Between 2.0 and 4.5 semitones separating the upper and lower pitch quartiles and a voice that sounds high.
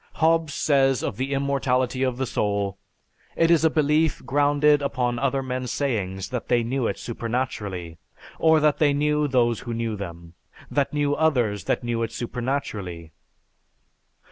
No: average, 4.0 semitones; low, 130 Hz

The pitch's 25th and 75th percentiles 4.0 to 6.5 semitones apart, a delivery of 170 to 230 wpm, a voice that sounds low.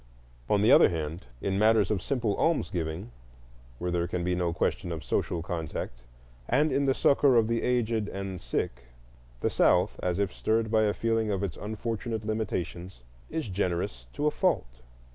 Yes: average, 4.6 semitones; average, 175 wpm; low, 100 Hz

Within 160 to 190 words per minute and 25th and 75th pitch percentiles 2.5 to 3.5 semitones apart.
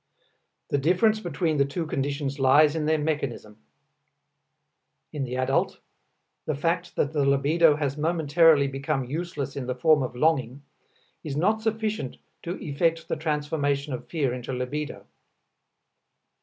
No: average, 140 wpm; average, 3.0 semitones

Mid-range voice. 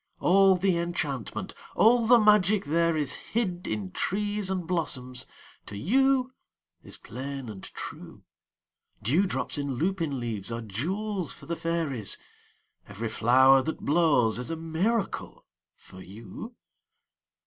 Yes: medium, 160 Hz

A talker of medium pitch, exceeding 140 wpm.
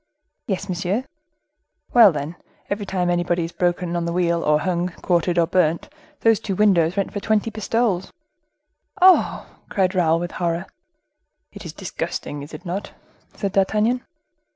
Yes: medium, 180 Hz; average, 155 wpm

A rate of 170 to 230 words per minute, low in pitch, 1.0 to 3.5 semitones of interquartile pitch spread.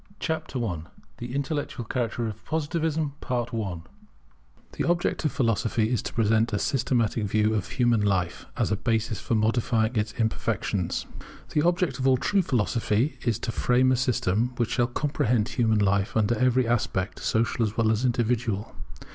No: average, 160 wpm; low, 115 Hz; average, 2.9 semitones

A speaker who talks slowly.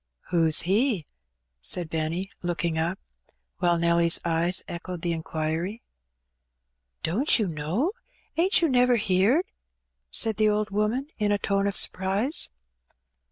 Yes: slow, 130 wpm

